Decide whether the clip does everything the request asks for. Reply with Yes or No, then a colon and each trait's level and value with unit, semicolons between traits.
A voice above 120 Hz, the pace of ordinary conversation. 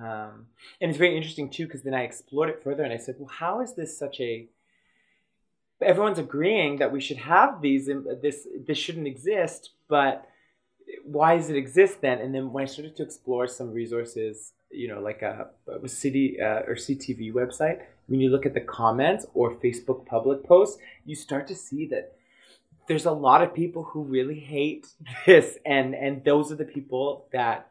Yes: medium, 140 Hz; average, 190 wpm